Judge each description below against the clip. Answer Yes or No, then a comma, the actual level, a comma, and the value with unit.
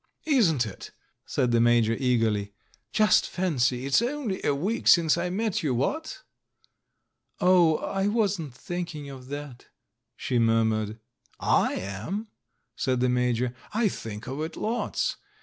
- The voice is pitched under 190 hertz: Yes, medium, 140 Hz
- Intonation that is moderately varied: No, wide, 7.9 semitones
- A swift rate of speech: No, slow, 135 wpm